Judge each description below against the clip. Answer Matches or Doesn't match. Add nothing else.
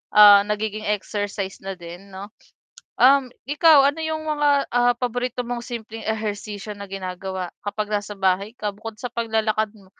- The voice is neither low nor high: Doesn't match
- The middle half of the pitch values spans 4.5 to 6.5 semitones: Doesn't match